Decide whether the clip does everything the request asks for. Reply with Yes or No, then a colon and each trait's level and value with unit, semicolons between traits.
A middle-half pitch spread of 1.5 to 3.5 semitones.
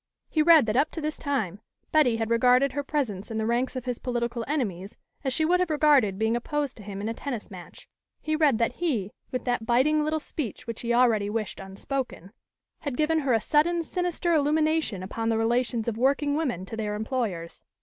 No: average, 5.2 semitones